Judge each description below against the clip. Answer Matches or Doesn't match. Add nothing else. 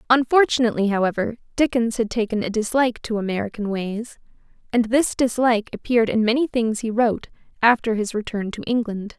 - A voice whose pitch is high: Matches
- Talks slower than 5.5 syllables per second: Doesn't match